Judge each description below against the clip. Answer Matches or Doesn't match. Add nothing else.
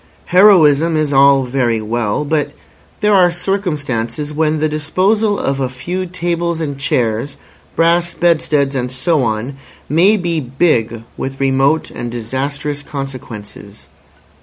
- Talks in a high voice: Doesn't match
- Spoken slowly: Matches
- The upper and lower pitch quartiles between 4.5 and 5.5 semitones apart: Matches